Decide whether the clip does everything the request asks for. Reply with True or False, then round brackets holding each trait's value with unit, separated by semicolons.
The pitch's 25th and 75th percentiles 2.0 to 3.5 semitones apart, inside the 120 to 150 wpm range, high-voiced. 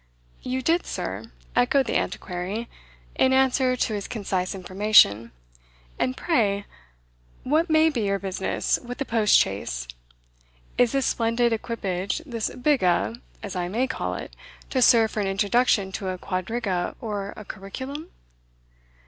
False (4.7 semitones; 140 wpm; 220 Hz)